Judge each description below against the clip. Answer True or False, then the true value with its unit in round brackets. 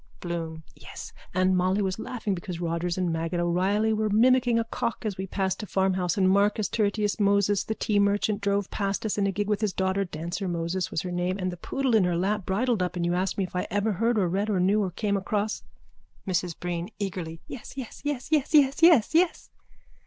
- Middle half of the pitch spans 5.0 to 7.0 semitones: False (3.0 semitones)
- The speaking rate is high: True (220 wpm)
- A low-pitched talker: False (195 Hz)